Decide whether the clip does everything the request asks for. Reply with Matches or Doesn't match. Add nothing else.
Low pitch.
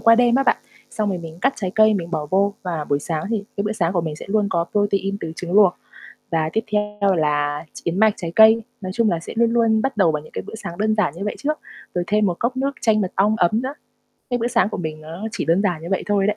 Doesn't match